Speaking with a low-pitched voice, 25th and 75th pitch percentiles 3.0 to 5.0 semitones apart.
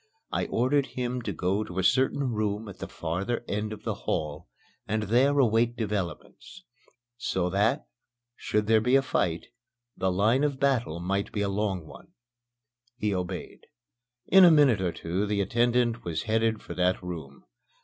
Yes: low, 105 Hz; average, 4.6 semitones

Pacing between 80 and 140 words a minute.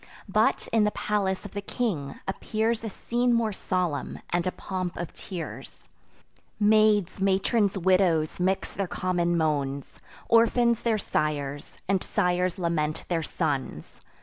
Yes: slow, 135 wpm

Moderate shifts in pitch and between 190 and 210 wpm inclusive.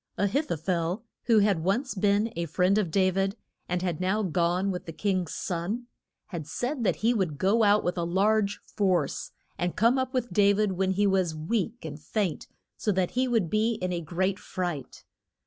Yes: average, 3.4 semitones; fast, 205 wpm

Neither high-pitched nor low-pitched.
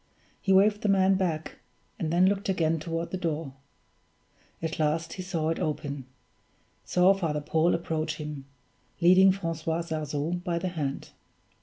Yes: medium, 165 Hz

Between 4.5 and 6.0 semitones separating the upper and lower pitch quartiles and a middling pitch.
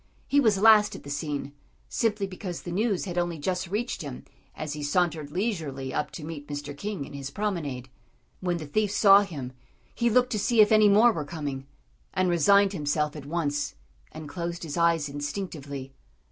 Yes: wide, 5.6 semitones; medium, 170 Hz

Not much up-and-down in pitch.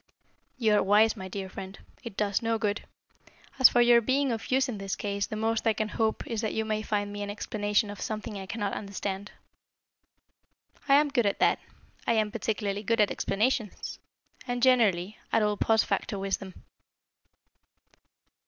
Yes: narrow, 2.1 semitones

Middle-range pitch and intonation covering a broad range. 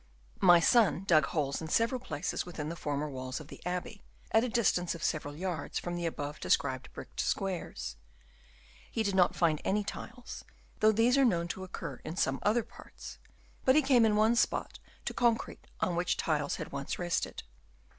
Yes: medium, 180 Hz; wide, 6.2 semitones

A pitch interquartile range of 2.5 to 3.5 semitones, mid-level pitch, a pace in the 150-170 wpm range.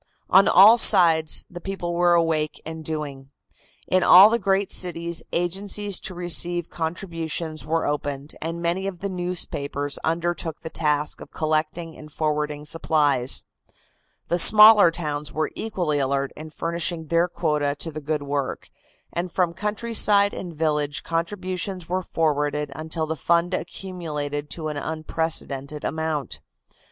No: average, 2.8 semitones; medium, 165 Hz; average, 140 wpm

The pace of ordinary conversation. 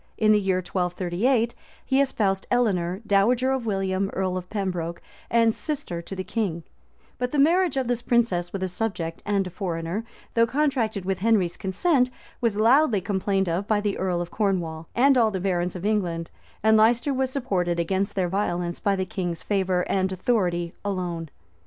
Yes: average, 175 wpm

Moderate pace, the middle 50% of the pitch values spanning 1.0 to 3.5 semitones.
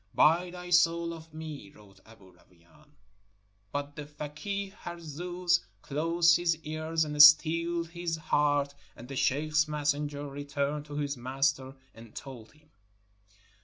No: slow, 130 wpm; average, 2.9 semitones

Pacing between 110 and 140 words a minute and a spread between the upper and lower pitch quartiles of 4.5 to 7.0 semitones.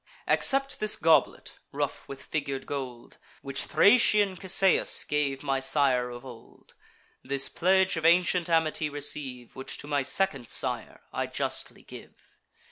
Yes: slow, 135 wpm; average, 5.1 semitones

